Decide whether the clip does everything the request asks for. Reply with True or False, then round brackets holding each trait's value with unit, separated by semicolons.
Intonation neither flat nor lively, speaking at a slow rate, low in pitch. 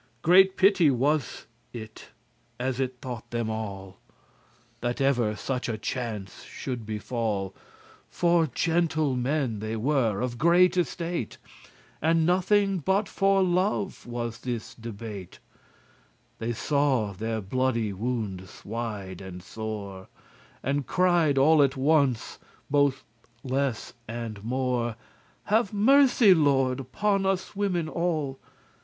False (6.9 semitones; 115 wpm; 130 Hz)